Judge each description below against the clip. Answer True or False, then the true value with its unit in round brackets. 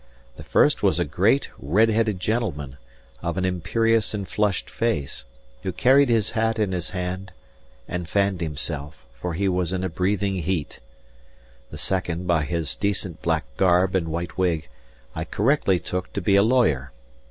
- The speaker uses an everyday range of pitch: True (3.5 semitones)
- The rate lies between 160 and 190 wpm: True (165 wpm)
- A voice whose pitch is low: True (90 Hz)